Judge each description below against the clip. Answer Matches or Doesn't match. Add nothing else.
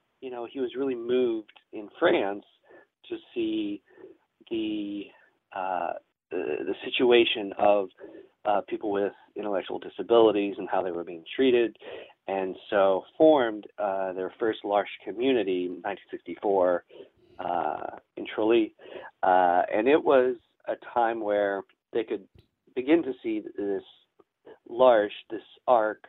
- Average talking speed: Doesn't match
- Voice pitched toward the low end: Matches